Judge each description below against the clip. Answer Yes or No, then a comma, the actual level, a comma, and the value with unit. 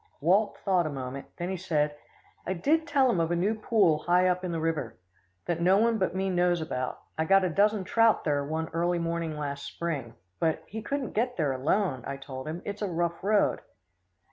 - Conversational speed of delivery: No, fast, 215 wpm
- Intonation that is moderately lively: Yes, average, 4.2 semitones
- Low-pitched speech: No, medium, 175 Hz